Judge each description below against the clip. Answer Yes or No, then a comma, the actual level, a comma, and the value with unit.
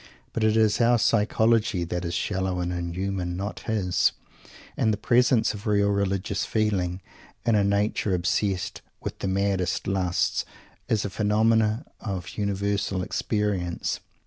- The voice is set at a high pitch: No, low, 100 Hz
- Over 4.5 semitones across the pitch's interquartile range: No, average, 2.8 semitones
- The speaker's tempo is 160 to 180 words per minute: No, average, 140 wpm